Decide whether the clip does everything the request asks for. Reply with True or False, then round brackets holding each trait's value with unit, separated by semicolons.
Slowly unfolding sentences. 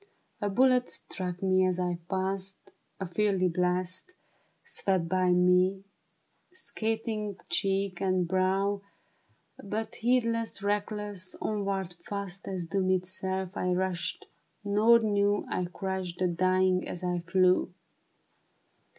True (115 wpm)